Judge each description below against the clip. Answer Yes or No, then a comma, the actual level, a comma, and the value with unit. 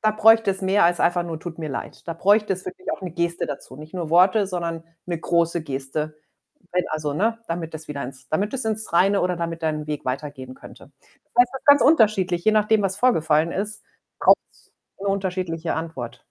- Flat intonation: No, average, 4.1 semitones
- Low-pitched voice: No, medium, 175 Hz